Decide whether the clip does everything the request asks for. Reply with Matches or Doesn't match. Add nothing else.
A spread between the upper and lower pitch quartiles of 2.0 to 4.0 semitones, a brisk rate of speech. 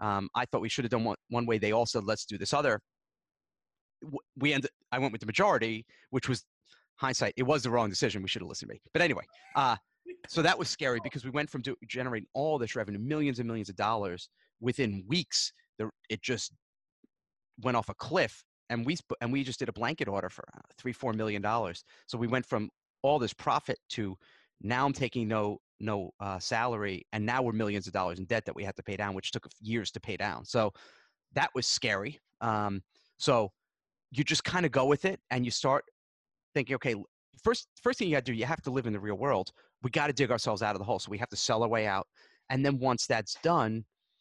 Doesn't match